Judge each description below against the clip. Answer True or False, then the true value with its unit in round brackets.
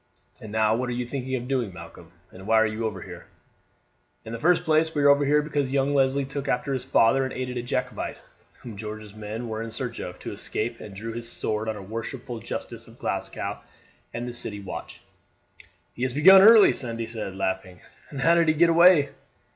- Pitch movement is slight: False (4.2 semitones)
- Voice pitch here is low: True (120 Hz)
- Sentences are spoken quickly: True (215 wpm)